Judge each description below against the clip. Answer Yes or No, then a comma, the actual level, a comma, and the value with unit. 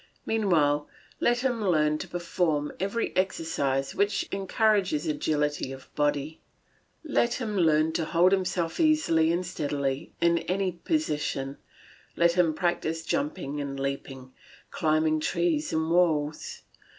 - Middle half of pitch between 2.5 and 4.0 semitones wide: No, average, 4.6 semitones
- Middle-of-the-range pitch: Yes, medium, 165 Hz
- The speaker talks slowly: Yes, slow, 125 wpm